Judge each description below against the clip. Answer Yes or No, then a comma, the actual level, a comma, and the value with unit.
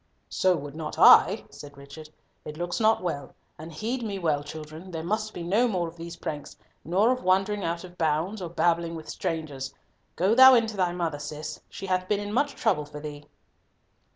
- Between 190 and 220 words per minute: Yes, fast, 205 wpm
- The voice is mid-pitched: Yes, medium, 170 Hz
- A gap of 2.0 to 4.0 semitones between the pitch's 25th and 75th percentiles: No, average, 4.4 semitones